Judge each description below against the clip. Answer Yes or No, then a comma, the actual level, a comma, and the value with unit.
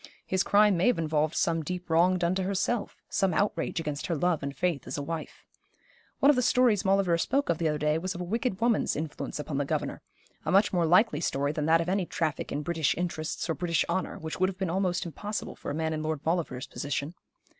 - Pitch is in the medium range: Yes, medium, 170 Hz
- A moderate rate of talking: No, fast, 235 wpm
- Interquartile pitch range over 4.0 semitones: No, average, 3.5 semitones